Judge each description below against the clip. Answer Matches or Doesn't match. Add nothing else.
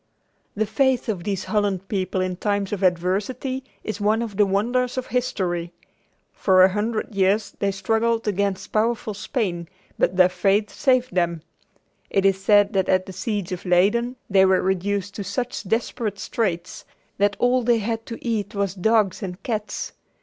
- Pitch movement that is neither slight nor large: Matches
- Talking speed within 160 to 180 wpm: Matches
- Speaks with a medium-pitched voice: Doesn't match